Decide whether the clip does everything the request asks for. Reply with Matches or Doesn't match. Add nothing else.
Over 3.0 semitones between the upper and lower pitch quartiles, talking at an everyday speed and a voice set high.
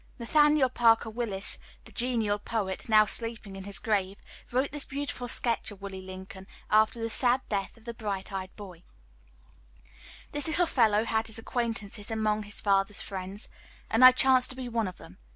Matches